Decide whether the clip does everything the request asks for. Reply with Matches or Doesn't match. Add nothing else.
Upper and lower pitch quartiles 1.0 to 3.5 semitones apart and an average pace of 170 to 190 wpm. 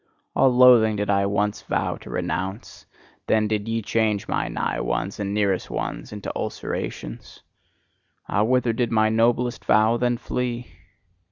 Doesn't match